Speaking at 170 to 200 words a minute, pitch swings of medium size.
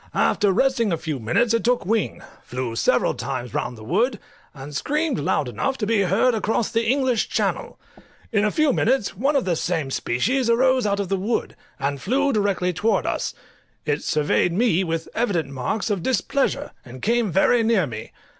No: average, 185 wpm; wide, 7.1 semitones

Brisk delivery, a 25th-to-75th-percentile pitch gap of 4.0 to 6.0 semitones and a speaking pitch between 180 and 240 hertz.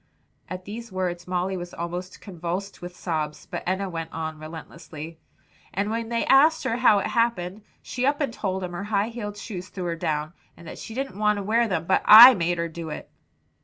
Yes: fast, 210 wpm; average, 4.3 semitones; medium, 185 Hz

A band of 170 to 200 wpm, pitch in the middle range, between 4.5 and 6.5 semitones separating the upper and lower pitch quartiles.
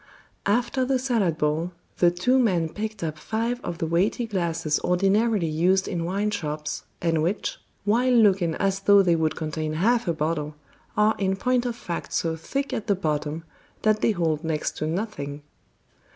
Yes: average, 175 wpm; medium, 180 Hz; average, 5.1 semitones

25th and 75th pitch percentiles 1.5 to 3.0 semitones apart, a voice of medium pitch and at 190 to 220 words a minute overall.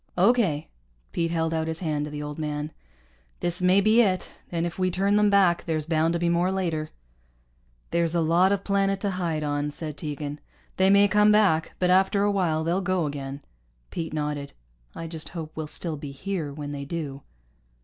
No: average, 3.7 semitones; medium, 165 Hz; average, 200 wpm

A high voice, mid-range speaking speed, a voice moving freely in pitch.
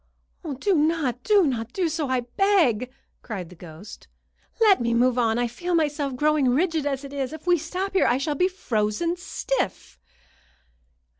Yes: very high, 285 Hz; average, 170 wpm; wide, 6.1 semitones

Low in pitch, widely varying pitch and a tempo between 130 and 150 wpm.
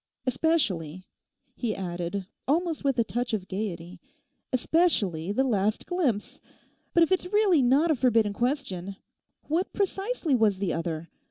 No: high, 240 Hz; wide, 8.8 semitones; average, 140 wpm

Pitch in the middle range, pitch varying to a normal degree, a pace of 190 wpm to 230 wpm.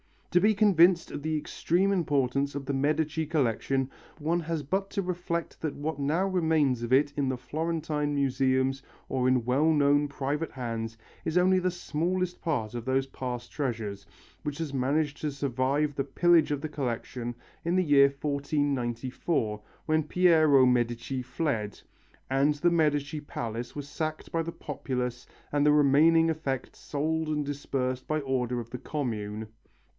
No: medium, 145 Hz; average, 3.6 semitones; average, 160 wpm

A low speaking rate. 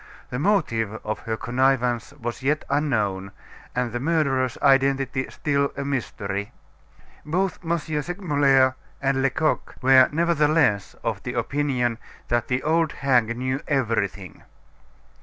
Yes: slow, 120 wpm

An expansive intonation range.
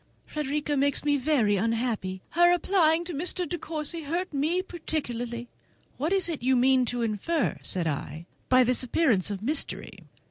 Yes: wide, 5.7 semitones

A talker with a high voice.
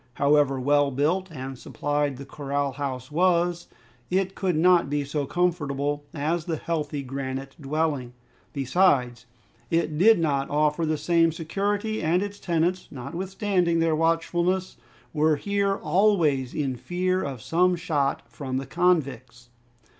No: medium, 155 Hz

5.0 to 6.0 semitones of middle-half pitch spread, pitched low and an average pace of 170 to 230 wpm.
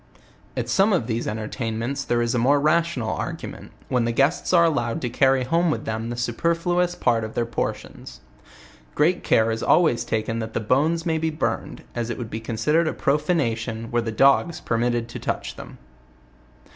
Yes: wide, 5.5 semitones; low, 120 Hz; average, 185 wpm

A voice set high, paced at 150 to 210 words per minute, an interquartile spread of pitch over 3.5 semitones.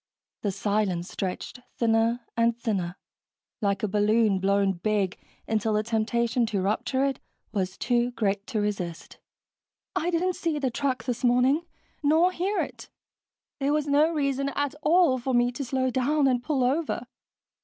Yes: high, 240 Hz; average, 155 wpm; average, 4.9 semitones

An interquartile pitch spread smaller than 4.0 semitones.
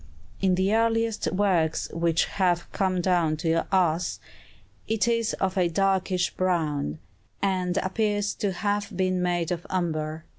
Yes: average, 2.8 semitones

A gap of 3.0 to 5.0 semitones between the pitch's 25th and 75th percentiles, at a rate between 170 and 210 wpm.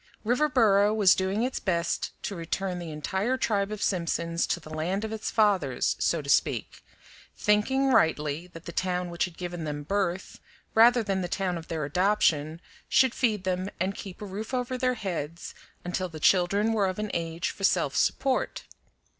Yes: average, 3.9 semitones; average, 180 wpm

